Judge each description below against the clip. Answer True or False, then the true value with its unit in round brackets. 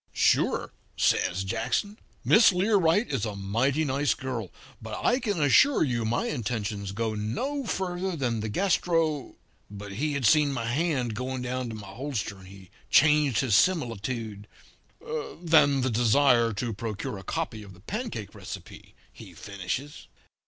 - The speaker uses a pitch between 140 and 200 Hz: False (125 Hz)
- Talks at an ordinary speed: True (150 wpm)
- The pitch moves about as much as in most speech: False (6.8 semitones)